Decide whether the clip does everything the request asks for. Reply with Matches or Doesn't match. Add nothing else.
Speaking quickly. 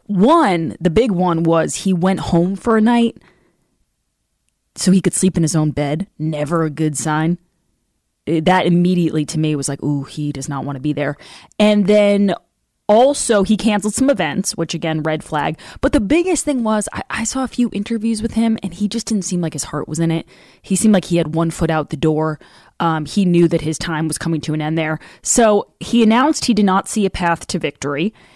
Matches